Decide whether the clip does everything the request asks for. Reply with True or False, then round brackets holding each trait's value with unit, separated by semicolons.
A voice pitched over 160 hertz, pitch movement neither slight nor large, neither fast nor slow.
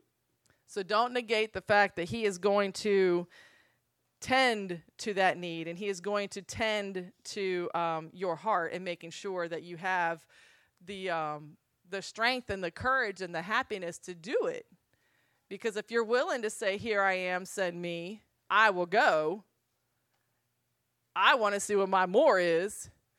True (190 Hz; 3.5 semitones; 170 wpm)